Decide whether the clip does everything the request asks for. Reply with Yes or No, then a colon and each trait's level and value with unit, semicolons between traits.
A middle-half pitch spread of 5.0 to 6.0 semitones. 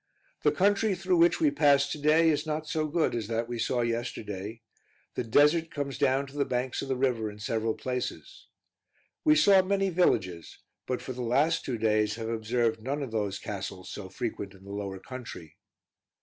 Yes: wide, 5.6 semitones